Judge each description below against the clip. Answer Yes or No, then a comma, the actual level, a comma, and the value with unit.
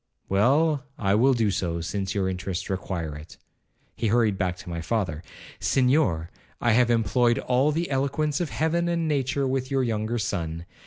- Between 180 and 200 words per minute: No, average, 170 wpm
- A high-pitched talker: No, low, 115 Hz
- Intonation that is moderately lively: No, wide, 6.3 semitones